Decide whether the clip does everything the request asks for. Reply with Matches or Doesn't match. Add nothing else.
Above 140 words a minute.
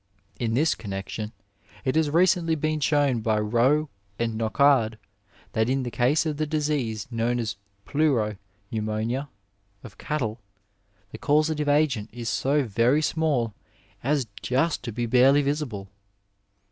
Doesn't match